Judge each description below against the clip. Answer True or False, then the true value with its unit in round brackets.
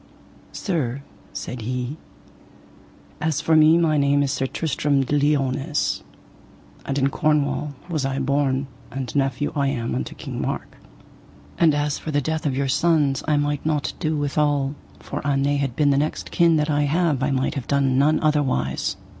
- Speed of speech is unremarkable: True (175 wpm)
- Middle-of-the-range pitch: True (145 Hz)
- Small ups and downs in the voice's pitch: True (1.9 semitones)